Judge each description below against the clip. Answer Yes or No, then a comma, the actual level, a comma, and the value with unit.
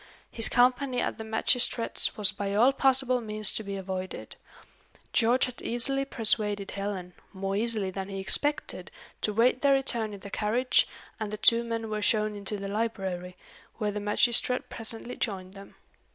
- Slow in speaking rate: No, average, 165 wpm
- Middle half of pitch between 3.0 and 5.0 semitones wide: Yes, average, 3.3 semitones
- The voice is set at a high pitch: Yes, high, 215 Hz